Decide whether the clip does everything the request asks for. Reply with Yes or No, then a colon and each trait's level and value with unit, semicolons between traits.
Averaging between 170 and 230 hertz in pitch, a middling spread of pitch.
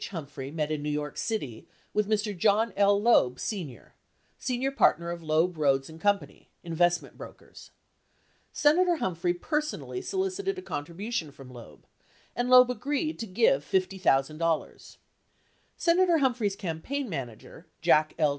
No: high, 190 Hz; wide, 8.4 semitones